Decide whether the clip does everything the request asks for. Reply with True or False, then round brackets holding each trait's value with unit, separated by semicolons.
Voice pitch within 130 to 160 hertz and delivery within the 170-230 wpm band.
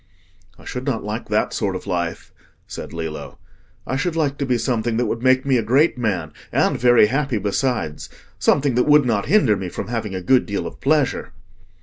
False (120 Hz; 200 wpm)